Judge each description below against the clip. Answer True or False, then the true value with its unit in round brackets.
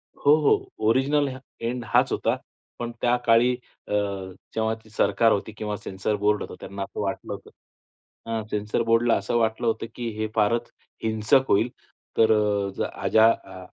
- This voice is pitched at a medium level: False (110 Hz)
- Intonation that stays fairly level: True (2.2 semitones)